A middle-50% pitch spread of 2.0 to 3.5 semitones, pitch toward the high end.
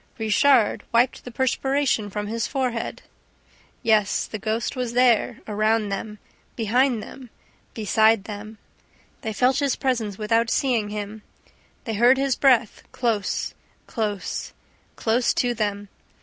Yes: average, 2.9 semitones; high, 225 Hz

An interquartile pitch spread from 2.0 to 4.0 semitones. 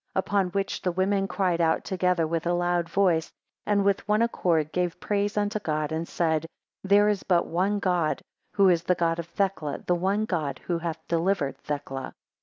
Yes: average, 3.1 semitones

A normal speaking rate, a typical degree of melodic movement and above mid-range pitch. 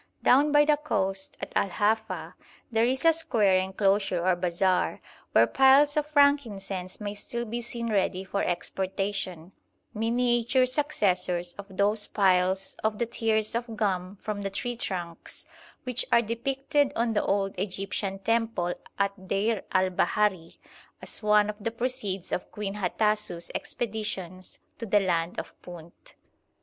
Yes: average, 145 wpm; average, 3.8 semitones; high, 205 Hz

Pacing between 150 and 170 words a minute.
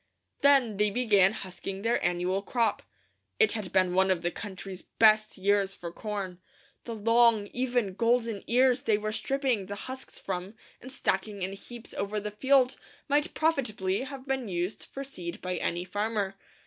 Yes: average, 165 wpm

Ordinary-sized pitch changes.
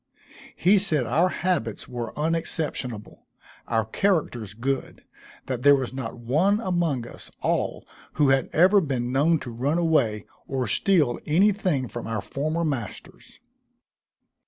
No: wide, 5.8 semitones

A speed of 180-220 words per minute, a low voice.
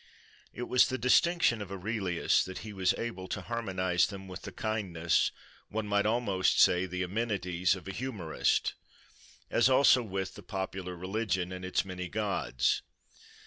No: average, 155 wpm; very low, 95 Hz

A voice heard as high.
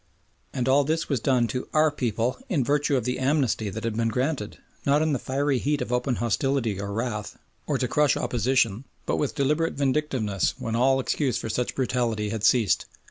No: low, 125 Hz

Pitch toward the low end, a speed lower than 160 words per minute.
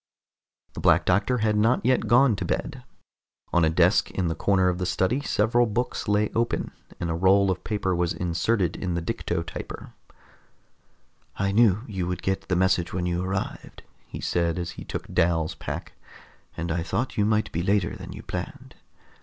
No: very low, 95 Hz; average, 185 wpm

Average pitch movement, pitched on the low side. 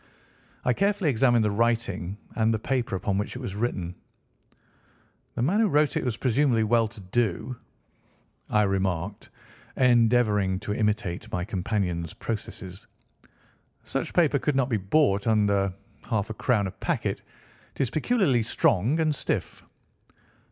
Yes: average, 4.2 semitones; low, 110 Hz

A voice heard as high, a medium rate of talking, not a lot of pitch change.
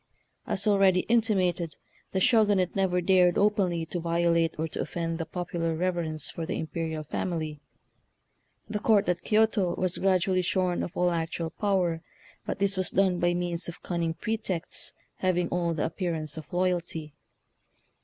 No: medium, 175 Hz; average, 155 wpm; narrow, 2.2 semitones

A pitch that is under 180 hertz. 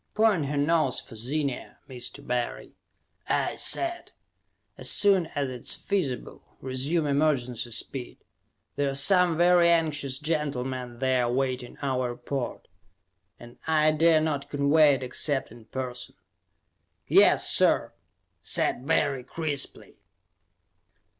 Yes: medium, 140 Hz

